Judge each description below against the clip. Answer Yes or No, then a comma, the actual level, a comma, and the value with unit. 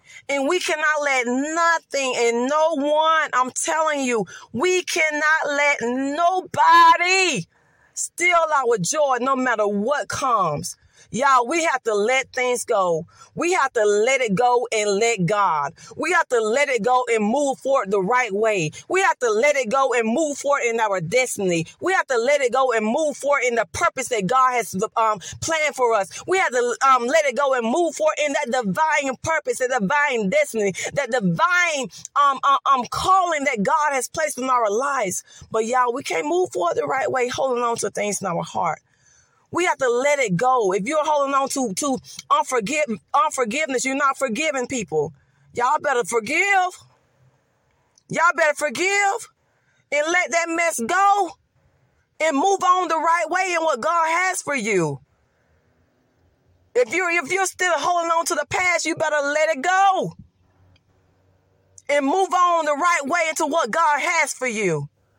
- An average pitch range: No, wide, 5.7 semitones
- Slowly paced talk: No, average, 180 wpm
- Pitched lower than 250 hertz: No, very high, 285 Hz